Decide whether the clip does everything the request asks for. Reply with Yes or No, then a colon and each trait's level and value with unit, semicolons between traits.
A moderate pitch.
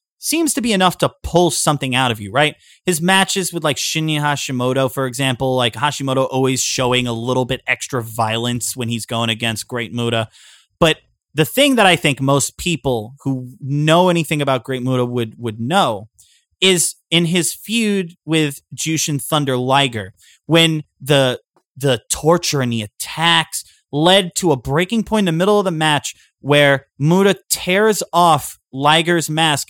Yes: medium, 145 Hz